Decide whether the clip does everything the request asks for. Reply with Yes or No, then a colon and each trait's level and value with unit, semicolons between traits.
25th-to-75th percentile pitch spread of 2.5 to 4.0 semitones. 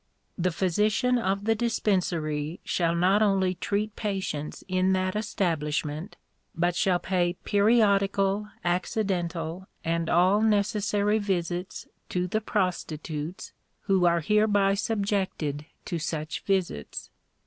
Yes: average, 3.3 semitones